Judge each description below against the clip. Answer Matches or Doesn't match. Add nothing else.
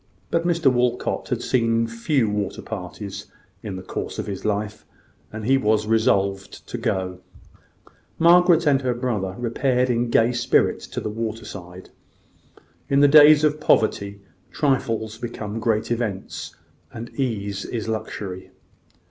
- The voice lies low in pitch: Matches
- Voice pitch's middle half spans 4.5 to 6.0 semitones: Doesn't match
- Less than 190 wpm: Matches